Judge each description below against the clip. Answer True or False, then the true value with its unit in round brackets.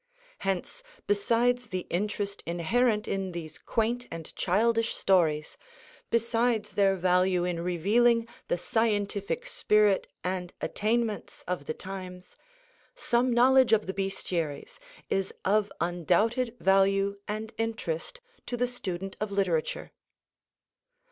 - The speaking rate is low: True (115 wpm)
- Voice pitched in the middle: False (200 Hz)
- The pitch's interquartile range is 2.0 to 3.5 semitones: False (4.2 semitones)